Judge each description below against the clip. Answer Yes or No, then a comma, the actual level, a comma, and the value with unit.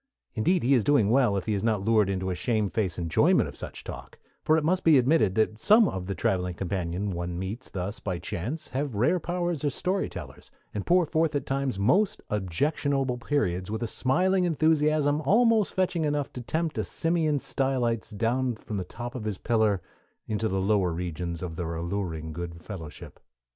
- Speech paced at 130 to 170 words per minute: No, average, 190 wpm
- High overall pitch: No, low, 115 Hz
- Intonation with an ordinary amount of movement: No, wide, 7.8 semitones